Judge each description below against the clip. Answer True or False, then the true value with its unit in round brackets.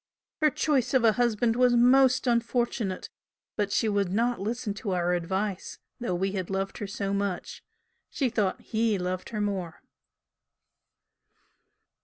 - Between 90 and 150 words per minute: True (145 wpm)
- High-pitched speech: True (210 Hz)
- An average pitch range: True (3.8 semitones)